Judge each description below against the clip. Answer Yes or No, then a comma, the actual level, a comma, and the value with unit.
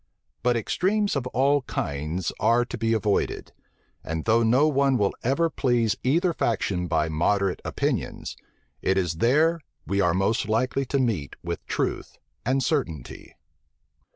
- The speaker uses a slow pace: No, average, 145 wpm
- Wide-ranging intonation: Yes, wide, 6.3 semitones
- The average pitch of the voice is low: Yes, low, 115 Hz